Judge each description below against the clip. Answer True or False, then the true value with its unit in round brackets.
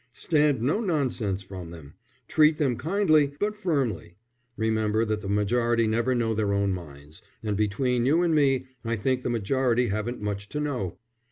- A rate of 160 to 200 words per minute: True (170 wpm)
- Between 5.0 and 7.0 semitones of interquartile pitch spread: True (5.4 semitones)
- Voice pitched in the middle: False (115 Hz)